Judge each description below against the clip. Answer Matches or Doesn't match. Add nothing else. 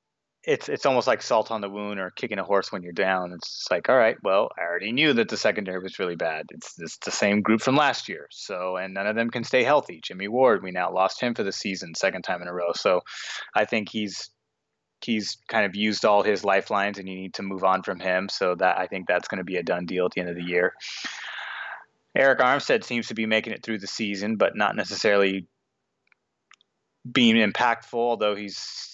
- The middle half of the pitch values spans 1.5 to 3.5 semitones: Matches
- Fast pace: Matches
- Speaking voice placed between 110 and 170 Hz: Doesn't match